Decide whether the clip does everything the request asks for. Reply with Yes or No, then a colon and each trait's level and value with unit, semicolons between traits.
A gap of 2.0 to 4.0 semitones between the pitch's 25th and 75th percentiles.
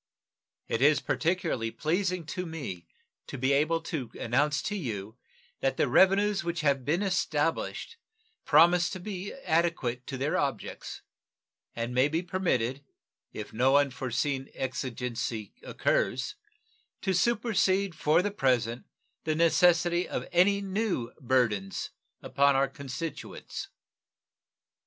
No: wide, 5.6 semitones